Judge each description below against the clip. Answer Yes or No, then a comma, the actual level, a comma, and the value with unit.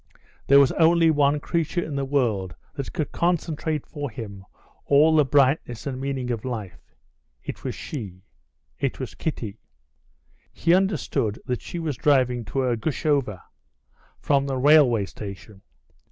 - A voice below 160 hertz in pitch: Yes, medium, 140 Hz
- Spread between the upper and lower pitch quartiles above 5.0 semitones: No, average, 4.7 semitones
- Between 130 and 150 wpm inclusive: Yes, average, 140 wpm